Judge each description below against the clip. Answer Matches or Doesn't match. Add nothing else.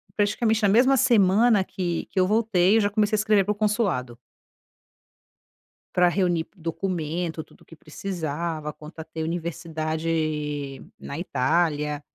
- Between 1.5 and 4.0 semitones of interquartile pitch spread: Doesn't match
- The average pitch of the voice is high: Doesn't match